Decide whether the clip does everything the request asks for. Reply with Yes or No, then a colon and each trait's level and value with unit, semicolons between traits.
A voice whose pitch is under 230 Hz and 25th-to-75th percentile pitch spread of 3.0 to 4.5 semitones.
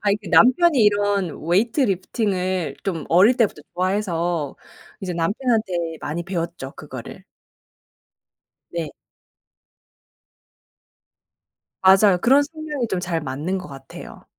Yes: high, 190 Hz; average, 4.0 semitones